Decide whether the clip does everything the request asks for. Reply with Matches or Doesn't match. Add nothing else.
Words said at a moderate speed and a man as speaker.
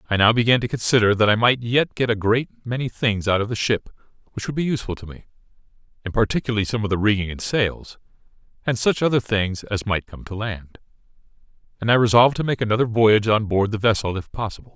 Doesn't match